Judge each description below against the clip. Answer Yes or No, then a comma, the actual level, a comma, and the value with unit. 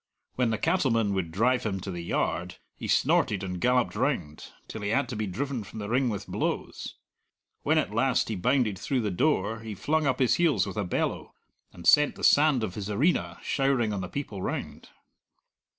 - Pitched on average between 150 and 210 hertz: No, low, 110 Hz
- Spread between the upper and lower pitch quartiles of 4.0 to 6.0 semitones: Yes, average, 5.2 semitones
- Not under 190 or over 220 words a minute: Yes, average, 200 wpm